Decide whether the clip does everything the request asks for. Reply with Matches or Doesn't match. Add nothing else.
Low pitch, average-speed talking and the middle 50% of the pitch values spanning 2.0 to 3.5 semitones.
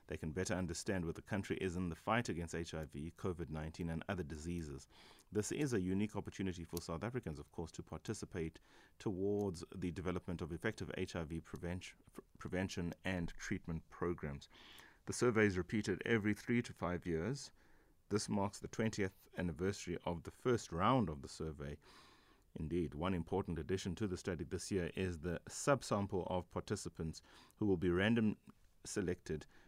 Matches